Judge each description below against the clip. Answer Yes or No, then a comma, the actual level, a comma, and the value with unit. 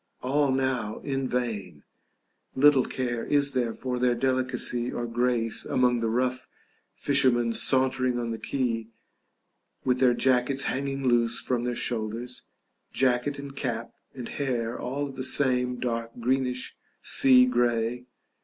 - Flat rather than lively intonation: Yes, narrow, 1.7 semitones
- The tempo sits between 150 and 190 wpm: No, slow, 135 wpm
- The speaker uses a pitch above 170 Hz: No, low, 125 Hz